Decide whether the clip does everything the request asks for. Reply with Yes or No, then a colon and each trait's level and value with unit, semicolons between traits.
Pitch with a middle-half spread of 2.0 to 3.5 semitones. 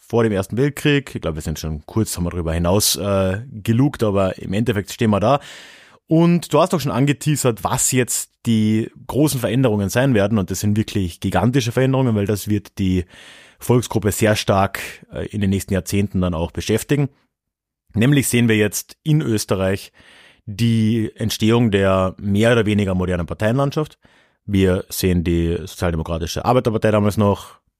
No: average, 4.2 semitones